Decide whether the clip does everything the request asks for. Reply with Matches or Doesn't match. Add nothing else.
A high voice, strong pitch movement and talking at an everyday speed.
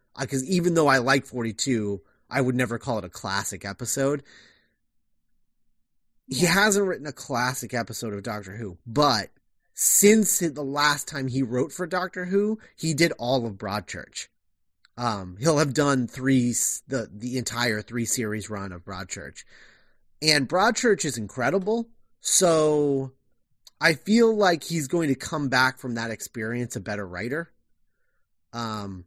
Doesn't match